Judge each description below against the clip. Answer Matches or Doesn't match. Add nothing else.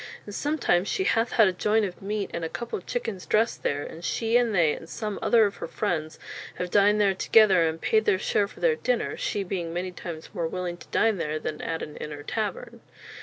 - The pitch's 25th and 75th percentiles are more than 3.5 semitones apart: Matches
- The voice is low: Doesn't match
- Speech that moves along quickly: Matches